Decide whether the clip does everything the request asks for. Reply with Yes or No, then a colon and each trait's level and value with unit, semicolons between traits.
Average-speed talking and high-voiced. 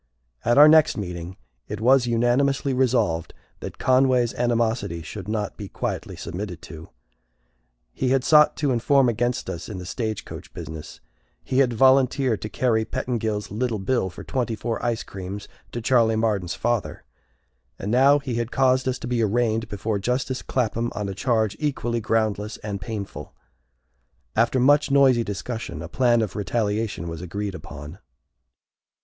No: average, 155 wpm; low, 115 Hz